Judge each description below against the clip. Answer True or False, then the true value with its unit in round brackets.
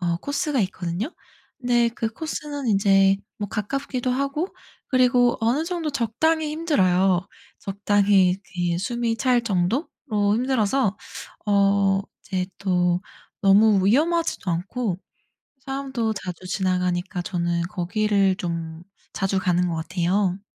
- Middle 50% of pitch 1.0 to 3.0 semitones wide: False (5.5 semitones)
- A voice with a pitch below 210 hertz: True (200 Hz)